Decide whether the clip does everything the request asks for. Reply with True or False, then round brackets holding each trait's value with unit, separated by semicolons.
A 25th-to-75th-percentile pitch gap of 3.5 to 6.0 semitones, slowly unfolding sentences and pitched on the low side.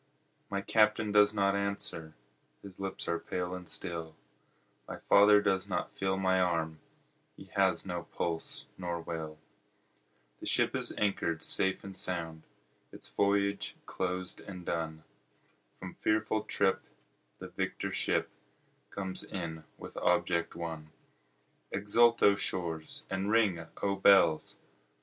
False (3.0 semitones; 130 wpm; 95 Hz)